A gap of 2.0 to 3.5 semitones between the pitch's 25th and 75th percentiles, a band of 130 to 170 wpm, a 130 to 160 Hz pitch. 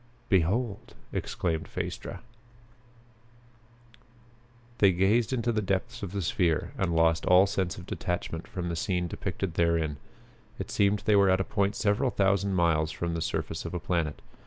No: average, 3.0 semitones; average, 160 wpm; very low, 95 Hz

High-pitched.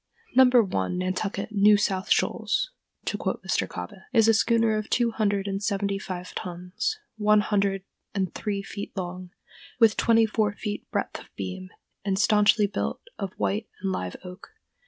Yes: high, 200 Hz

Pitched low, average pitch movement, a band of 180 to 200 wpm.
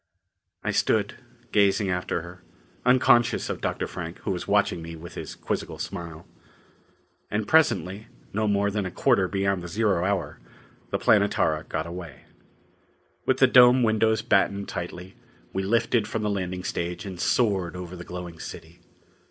No: very low, 95 Hz; average, 3.4 semitones; average, 155 wpm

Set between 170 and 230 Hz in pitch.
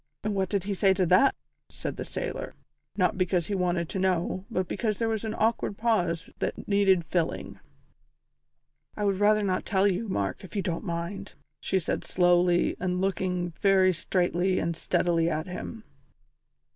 Yes: medium, 185 Hz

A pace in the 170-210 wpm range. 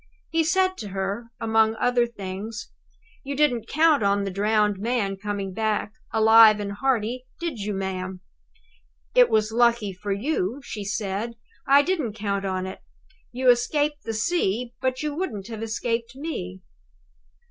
No: average, 150 wpm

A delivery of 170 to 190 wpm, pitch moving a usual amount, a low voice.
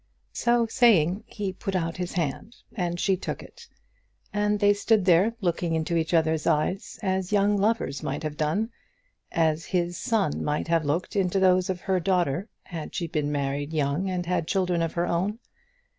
No: average, 180 wpm; average, 3.7 semitones; medium, 180 Hz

